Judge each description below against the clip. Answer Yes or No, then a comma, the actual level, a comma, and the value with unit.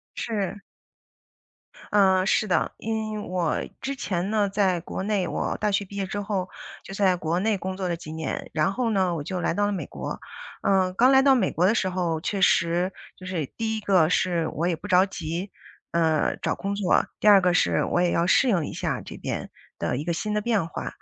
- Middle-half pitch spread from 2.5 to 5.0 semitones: Yes, average, 3.0 semitones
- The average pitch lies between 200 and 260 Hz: No, high, 190 Hz